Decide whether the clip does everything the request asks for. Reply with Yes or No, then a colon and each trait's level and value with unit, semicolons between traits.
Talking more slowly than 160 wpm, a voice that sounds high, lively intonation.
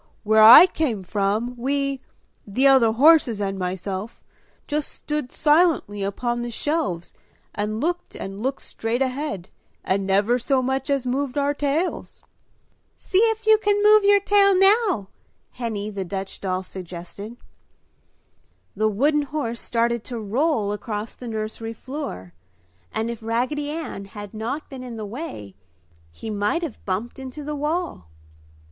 Yes: average, 145 wpm; high, 240 Hz; wide, 6.2 semitones